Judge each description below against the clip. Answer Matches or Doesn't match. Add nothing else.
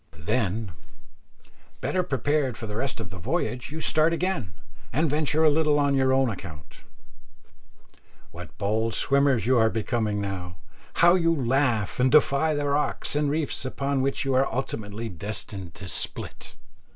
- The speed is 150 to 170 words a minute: Matches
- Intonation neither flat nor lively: Doesn't match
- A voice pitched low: Matches